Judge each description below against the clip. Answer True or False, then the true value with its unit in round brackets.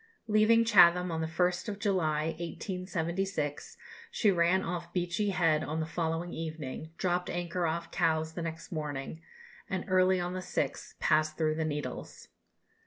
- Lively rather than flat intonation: False (2.4 semitones)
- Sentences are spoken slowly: False (150 wpm)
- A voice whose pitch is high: False (170 Hz)